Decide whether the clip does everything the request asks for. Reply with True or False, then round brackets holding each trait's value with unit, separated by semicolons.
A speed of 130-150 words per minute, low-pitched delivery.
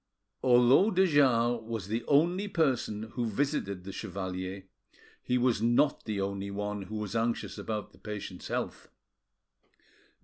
True (140 wpm; 115 Hz)